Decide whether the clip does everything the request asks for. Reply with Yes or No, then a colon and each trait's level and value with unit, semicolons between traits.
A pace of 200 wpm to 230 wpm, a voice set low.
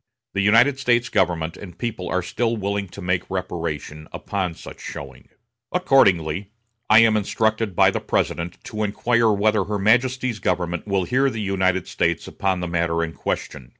No: average, 165 wpm; low, 100 Hz